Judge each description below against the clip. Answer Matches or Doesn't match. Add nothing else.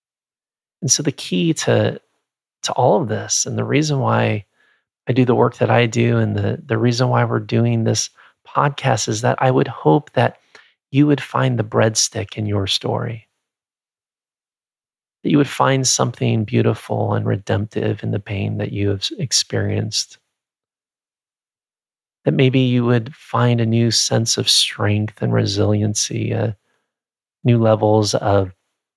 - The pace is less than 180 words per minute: Matches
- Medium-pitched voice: Doesn't match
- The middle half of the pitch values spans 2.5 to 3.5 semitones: Matches